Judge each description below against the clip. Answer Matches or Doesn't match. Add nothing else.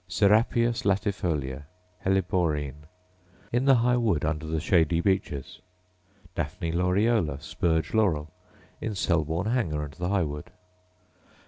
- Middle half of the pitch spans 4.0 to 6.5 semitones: Matches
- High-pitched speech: Doesn't match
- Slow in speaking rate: Matches